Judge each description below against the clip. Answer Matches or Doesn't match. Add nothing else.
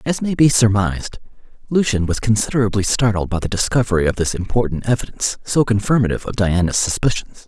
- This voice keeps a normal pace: Matches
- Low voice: Matches